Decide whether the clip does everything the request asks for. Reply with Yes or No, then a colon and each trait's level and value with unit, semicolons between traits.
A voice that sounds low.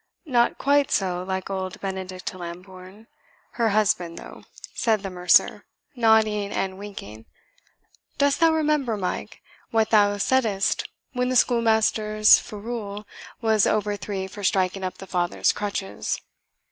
No: high, 205 Hz